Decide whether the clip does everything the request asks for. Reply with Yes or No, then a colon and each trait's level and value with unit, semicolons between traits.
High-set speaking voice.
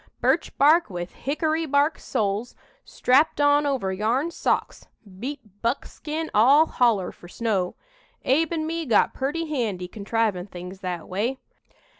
Yes: high, 245 Hz